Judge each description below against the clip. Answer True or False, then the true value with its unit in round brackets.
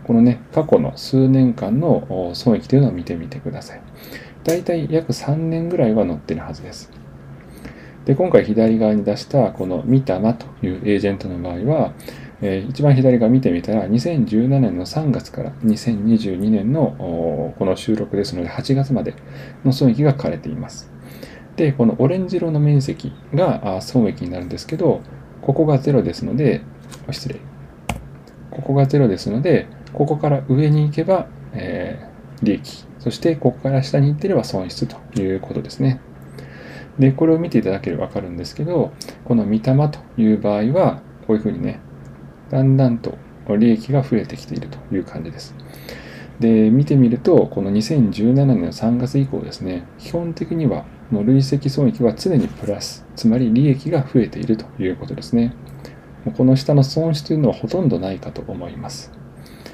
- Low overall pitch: True (125 Hz)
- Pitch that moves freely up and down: False (4.4 semitones)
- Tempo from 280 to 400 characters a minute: True (320 characters per minute)